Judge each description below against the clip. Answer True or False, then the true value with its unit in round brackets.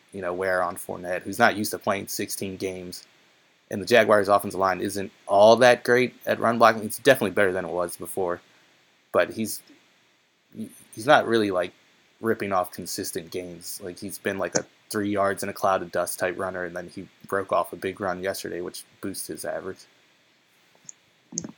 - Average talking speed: True (190 wpm)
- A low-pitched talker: True (95 Hz)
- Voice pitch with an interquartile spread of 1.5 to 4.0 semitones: True (2.8 semitones)